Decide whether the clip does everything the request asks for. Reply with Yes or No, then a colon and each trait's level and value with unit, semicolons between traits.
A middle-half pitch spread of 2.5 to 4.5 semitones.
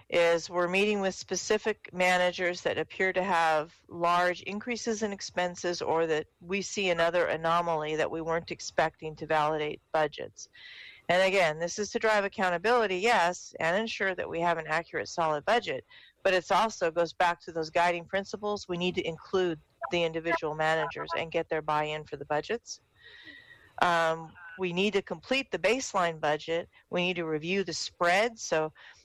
Yes: average, 3.3 semitones